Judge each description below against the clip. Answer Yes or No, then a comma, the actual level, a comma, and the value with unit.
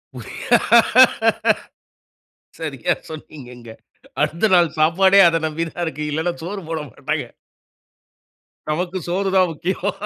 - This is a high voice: No, medium, 165 Hz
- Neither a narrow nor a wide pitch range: Yes, average, 3.1 semitones